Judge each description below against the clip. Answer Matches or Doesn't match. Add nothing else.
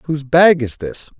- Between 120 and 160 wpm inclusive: Doesn't match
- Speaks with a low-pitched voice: Doesn't match